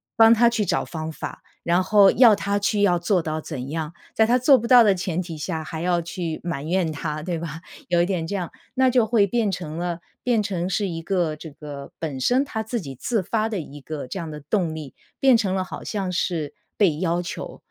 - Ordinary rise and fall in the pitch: Yes, average, 4.7 semitones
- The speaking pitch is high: No, medium, 180 Hz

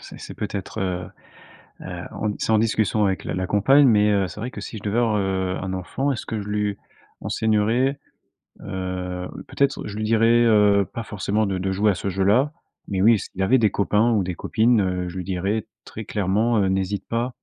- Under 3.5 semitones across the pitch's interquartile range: Yes, average, 2.8 semitones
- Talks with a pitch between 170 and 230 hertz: No, low, 105 Hz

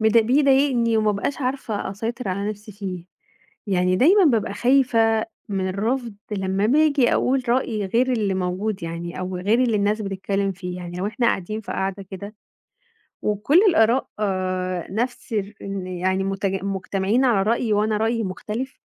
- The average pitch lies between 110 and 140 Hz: No, high, 210 Hz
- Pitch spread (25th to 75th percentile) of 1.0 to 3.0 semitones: No, average, 3.7 semitones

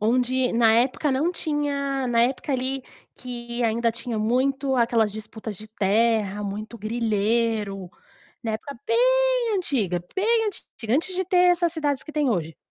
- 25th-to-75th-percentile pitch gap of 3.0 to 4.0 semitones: No, average, 4.9 semitones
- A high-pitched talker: Yes, high, 240 Hz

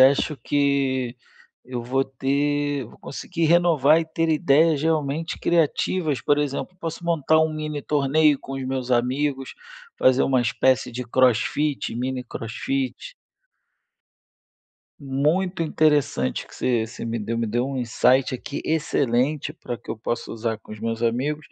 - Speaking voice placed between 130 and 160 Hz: Yes, medium, 140 Hz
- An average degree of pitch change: Yes, average, 3.7 semitones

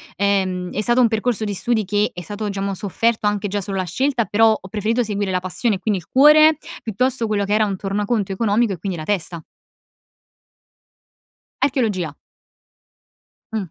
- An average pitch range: Yes, average, 3.0 semitones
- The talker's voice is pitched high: Yes, high, 205 Hz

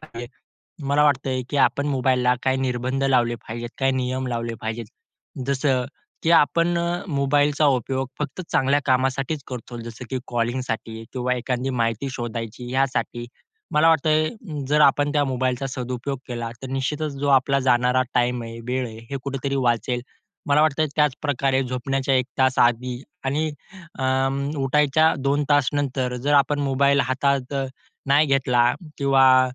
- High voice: No, low, 130 Hz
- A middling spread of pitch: No, narrow, 2.1 semitones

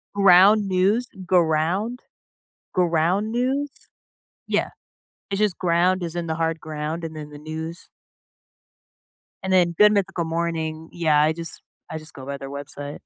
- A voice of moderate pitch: Yes, medium, 170 Hz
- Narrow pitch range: No, average, 3.2 semitones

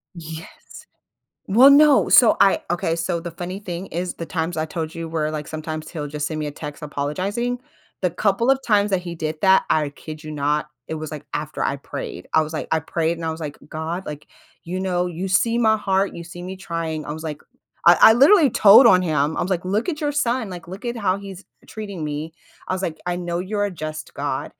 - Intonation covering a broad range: No, average, 3.9 semitones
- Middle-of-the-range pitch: Yes, medium, 175 Hz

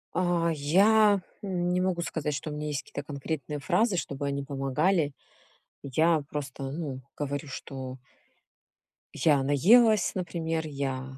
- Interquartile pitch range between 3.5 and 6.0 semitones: Yes, average, 4.0 semitones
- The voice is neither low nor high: Yes, medium, 150 Hz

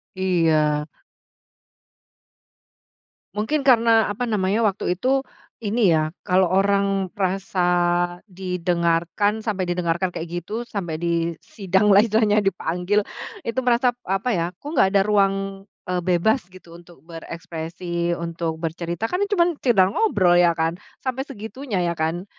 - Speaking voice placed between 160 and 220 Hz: Yes, medium, 185 Hz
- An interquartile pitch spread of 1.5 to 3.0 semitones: No, average, 3.6 semitones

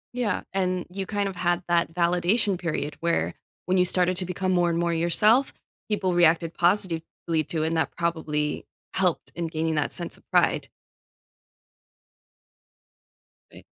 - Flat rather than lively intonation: Yes, narrow, 2.0 semitones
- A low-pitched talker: No, medium, 175 Hz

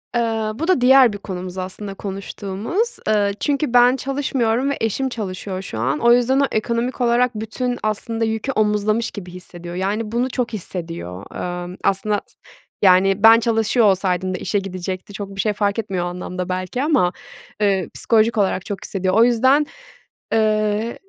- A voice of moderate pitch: No, high, 210 Hz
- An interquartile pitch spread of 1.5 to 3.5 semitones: No, average, 4.0 semitones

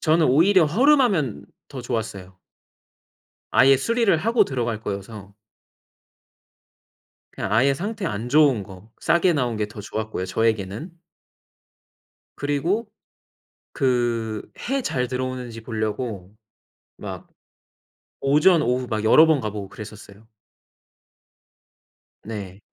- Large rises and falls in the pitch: Yes, wide, 6.4 semitones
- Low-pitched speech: Yes, low, 125 Hz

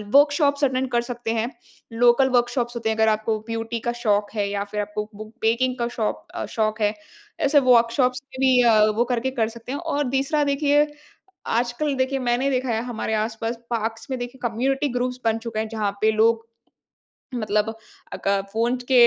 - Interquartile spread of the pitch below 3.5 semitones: Yes, average, 2.9 semitones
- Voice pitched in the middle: No, high, 235 Hz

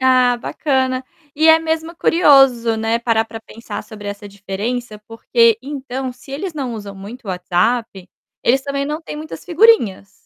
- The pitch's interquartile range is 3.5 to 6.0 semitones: Yes, average, 4.1 semitones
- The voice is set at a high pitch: Yes, high, 245 Hz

